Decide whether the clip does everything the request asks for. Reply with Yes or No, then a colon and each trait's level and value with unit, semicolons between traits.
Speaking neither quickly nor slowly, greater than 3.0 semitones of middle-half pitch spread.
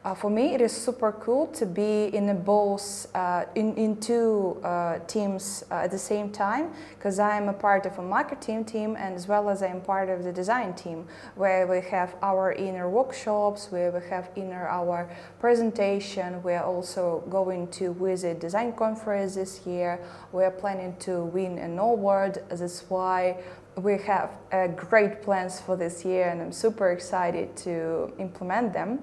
No: average, 185 wpm; narrow, 2.6 semitones